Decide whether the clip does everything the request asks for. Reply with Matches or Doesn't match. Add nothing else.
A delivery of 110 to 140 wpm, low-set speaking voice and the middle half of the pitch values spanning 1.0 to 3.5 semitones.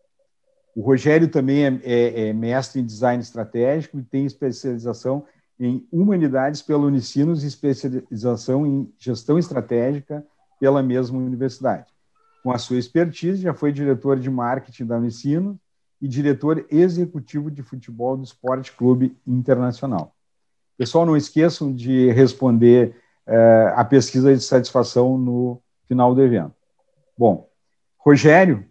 Matches